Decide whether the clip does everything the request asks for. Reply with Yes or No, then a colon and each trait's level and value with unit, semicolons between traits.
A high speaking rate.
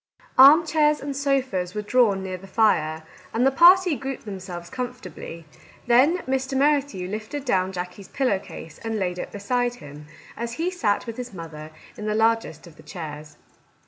No: average, 175 wpm